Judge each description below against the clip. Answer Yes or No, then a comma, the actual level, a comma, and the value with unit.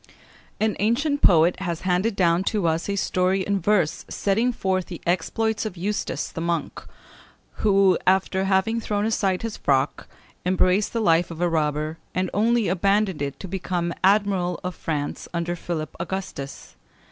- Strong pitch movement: No, average, 3.1 semitones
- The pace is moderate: Yes, average, 160 wpm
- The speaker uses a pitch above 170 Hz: Yes, medium, 185 Hz